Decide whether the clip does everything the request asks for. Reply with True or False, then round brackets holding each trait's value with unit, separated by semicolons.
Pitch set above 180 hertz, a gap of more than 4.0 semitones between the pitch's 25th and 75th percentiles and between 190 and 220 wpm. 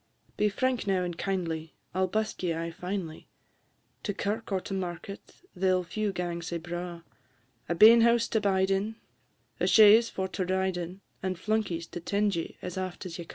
False (190 Hz; 2.9 semitones; 200 wpm)